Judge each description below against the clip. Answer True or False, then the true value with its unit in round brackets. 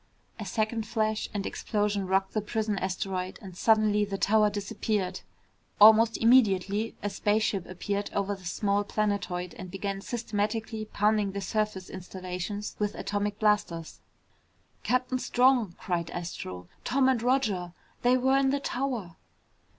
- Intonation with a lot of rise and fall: False (2.5 semitones)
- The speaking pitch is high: True (205 Hz)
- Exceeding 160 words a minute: False (135 wpm)